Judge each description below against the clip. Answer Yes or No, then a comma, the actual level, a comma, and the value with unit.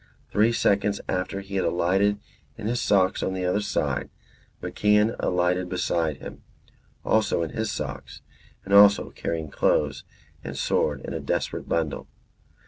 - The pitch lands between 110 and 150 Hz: No, very low, 95 Hz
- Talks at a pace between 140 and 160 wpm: Yes, average, 145 wpm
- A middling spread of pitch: Yes, average, 3.3 semitones